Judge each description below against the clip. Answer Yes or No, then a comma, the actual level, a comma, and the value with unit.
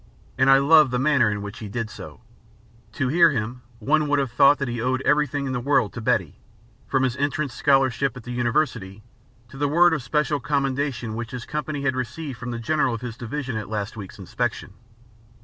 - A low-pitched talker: Yes, low, 130 Hz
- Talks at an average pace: No, fast, 210 wpm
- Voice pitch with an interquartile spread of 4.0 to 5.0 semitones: No, average, 3.5 semitones